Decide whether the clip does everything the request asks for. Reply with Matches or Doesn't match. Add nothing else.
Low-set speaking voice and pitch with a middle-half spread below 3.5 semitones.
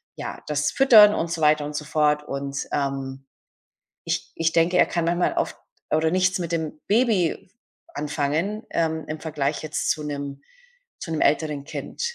Doesn't match